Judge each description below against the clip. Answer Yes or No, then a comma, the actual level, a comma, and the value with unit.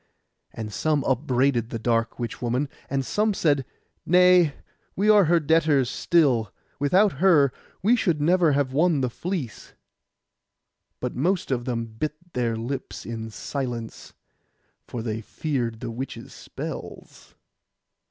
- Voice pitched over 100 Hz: Yes, low, 135 Hz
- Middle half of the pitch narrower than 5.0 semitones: No, wide, 5.6 semitones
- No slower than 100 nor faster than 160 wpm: Yes, slow, 135 wpm